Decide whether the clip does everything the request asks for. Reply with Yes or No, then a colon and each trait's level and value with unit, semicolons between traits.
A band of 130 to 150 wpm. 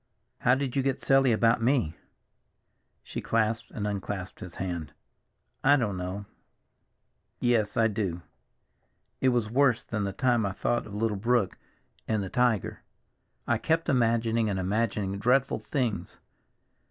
Yes: average, 140 wpm